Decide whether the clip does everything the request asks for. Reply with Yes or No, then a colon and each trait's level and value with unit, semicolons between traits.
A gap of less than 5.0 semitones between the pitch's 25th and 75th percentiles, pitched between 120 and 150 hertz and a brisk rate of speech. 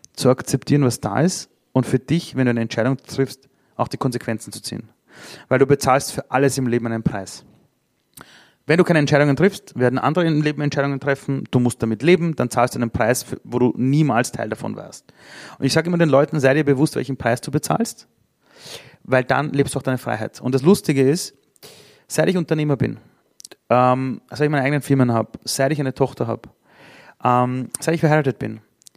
Yes: average, 3.0 semitones; low, 135 Hz; fast, 205 wpm